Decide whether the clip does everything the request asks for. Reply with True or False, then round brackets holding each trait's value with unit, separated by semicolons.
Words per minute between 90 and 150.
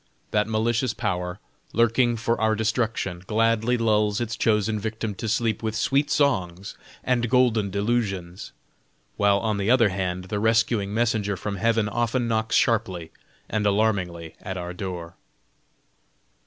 True (140 wpm)